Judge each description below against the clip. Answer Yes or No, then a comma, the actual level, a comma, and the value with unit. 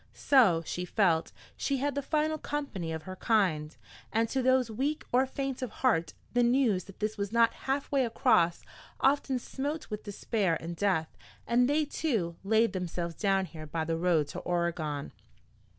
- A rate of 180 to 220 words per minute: No, average, 170 wpm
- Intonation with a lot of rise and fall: Yes, wide, 7.3 semitones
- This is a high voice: Yes, high, 215 Hz